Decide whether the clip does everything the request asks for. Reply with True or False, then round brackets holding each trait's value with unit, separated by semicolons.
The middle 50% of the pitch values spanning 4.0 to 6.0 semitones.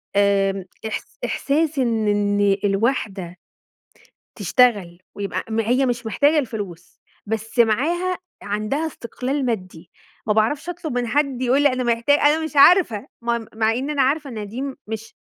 True (5.2 semitones)